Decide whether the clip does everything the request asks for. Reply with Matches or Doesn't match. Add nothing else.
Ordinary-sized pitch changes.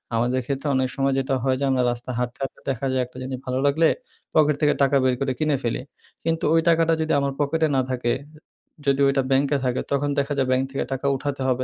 Doesn't match